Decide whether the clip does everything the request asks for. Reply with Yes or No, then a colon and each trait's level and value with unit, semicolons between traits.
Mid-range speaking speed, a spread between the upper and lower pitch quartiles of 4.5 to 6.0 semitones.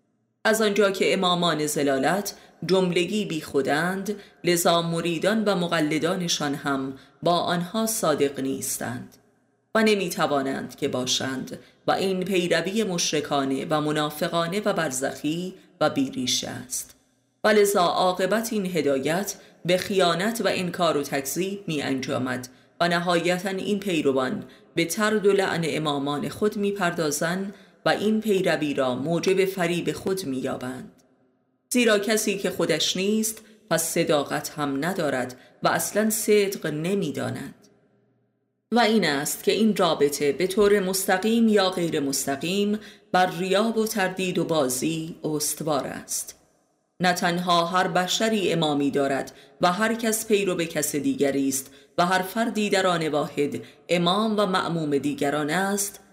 Yes: average, 135 wpm; average, 5.1 semitones